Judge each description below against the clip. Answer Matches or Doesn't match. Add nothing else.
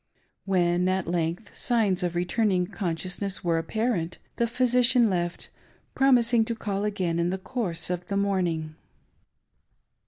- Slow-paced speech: Matches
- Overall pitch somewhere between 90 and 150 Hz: Doesn't match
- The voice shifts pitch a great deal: Doesn't match